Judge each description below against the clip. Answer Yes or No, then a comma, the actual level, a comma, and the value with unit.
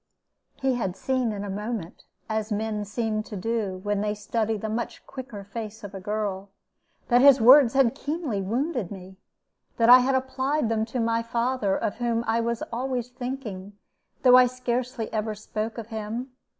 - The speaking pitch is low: No, high, 230 Hz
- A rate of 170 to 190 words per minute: Yes, average, 175 wpm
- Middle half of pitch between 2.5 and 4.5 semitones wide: Yes, average, 3.2 semitones